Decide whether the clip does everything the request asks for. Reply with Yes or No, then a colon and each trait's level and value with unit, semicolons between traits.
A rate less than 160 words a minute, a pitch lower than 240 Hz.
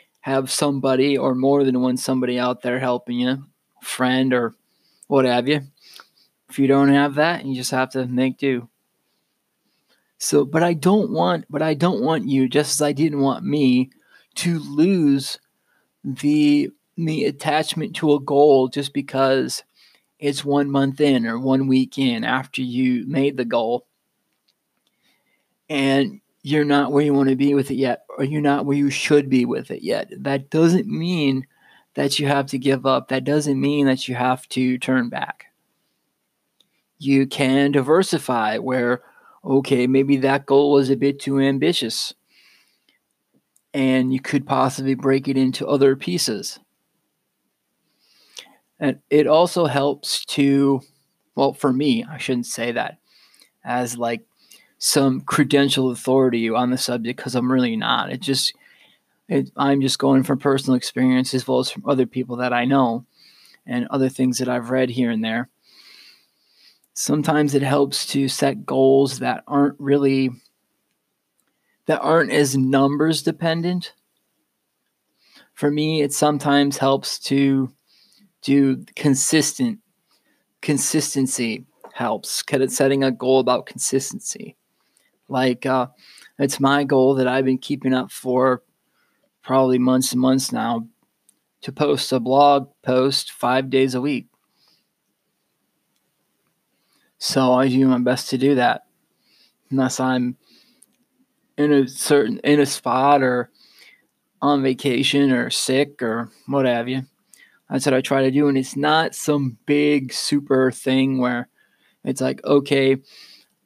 Yes: average, 145 wpm; low, 135 Hz